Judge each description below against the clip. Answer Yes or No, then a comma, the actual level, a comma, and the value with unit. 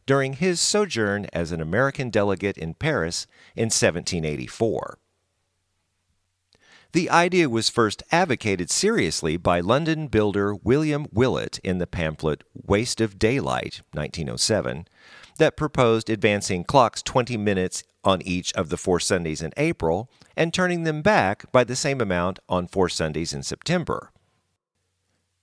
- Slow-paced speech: Yes, slow, 130 wpm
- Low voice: Yes, low, 100 Hz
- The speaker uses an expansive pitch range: Yes, wide, 6.0 semitones